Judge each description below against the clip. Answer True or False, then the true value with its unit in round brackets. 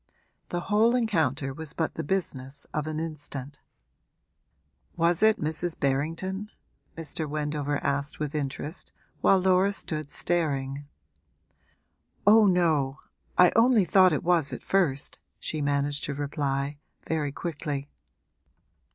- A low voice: False (155 Hz)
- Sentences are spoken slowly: True (120 wpm)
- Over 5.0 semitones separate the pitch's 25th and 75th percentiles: False (4.0 semitones)